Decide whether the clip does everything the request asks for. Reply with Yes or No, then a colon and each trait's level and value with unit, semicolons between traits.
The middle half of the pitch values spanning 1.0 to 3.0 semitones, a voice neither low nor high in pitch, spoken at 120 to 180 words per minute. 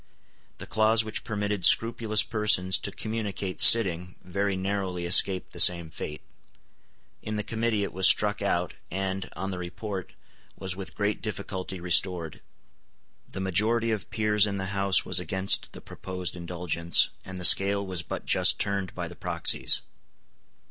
No: narrow, 2.4 semitones; very low, 95 Hz; average, 155 wpm